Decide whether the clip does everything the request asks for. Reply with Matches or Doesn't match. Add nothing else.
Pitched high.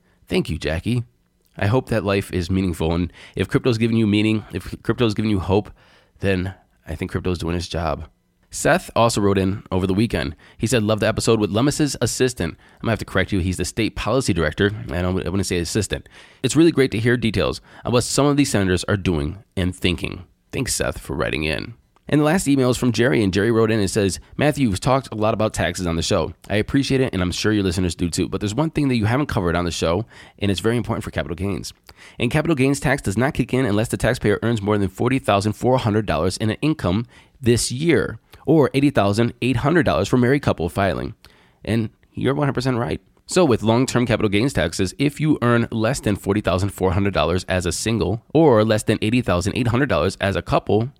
Doesn't match